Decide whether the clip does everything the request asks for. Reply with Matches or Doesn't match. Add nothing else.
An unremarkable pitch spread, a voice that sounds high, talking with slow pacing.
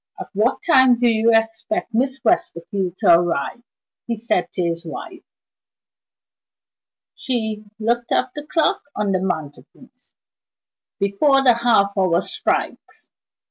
Matches